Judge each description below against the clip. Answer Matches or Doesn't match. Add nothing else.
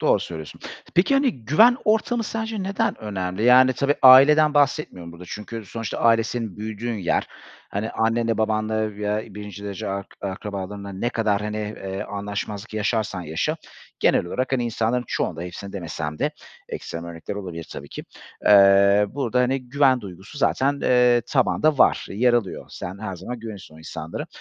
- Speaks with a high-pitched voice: Doesn't match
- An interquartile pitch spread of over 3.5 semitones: Matches